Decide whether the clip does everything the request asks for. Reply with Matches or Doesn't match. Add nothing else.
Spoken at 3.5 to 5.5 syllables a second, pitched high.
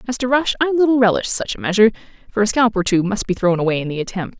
Doesn't match